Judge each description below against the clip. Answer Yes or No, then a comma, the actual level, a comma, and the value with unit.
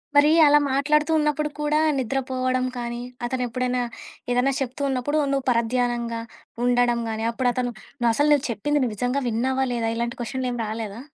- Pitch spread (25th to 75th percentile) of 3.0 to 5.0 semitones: No, narrow, 2.4 semitones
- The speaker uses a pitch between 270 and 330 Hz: No, very high, 250 Hz